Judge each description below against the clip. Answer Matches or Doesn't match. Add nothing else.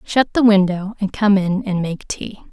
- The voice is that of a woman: Matches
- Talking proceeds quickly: Matches